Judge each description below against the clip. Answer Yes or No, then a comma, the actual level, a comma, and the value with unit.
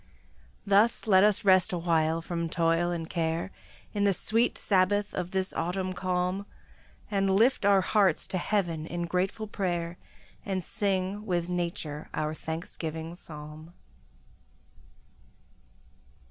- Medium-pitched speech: Yes, medium, 180 Hz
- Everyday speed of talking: No, slow, 120 wpm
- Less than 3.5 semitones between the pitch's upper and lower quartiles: Yes, average, 2.9 semitones